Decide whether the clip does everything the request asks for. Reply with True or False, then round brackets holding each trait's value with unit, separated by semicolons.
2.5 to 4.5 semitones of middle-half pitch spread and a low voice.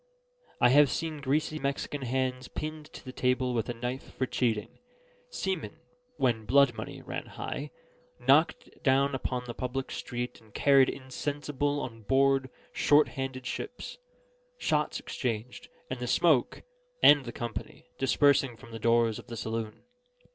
True (2.8 semitones; 130 Hz)